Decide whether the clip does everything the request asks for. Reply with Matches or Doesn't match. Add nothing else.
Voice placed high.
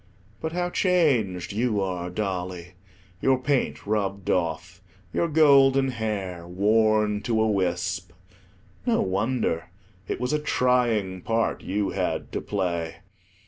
Doesn't match